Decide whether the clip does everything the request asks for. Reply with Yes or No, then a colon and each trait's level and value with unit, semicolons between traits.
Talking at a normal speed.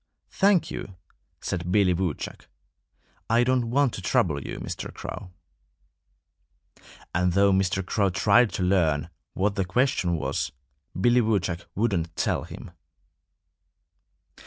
No: slow, 120 wpm